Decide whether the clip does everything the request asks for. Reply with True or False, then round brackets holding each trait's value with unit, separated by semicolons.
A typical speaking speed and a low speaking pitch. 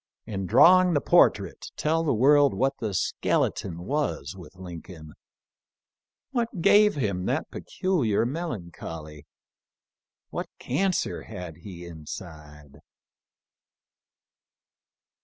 False (100 wpm; 100 Hz)